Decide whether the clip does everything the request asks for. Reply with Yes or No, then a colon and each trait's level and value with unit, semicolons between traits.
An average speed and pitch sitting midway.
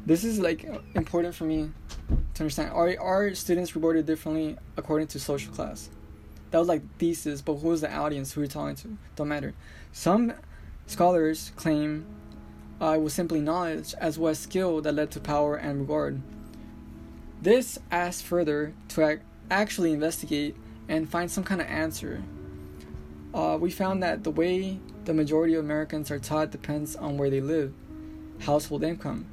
Yes: average, 165 wpm; medium, 155 Hz